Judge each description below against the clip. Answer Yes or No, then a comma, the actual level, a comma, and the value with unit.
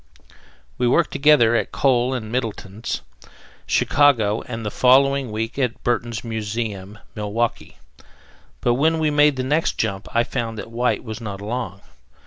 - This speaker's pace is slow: No, average, 145 wpm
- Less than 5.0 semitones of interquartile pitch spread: Yes, average, 3.2 semitones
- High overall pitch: No, low, 120 Hz